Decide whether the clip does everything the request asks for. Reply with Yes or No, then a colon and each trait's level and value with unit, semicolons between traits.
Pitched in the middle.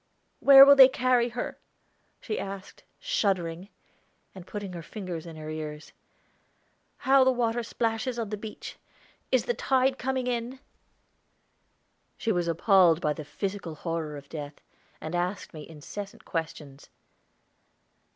No: high, 195 Hz